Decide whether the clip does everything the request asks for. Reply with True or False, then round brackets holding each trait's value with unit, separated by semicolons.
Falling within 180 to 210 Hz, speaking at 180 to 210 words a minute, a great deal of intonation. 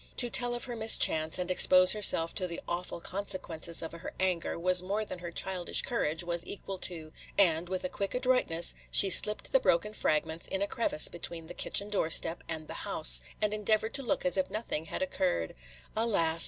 False (185 Hz; 195 wpm; 4.0 semitones)